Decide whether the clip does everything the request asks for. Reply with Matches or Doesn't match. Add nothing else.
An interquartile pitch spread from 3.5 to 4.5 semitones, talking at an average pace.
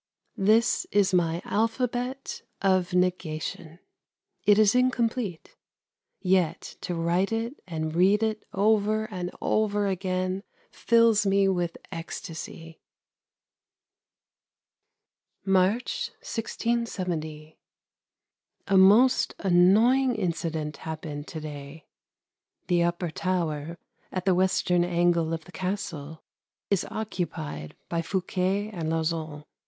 Doesn't match